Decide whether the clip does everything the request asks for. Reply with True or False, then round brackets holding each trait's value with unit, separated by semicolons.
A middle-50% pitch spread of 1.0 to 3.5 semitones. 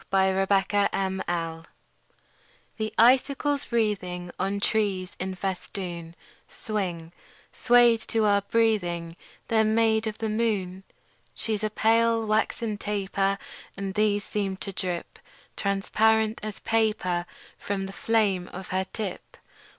True (2.7 semitones)